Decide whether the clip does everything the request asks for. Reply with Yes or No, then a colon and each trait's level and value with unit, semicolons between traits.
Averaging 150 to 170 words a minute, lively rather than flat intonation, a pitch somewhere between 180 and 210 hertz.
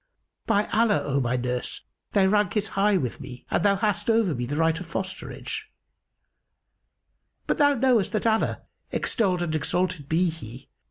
Yes: average, 165 wpm; wide, 5.8 semitones; medium, 185 Hz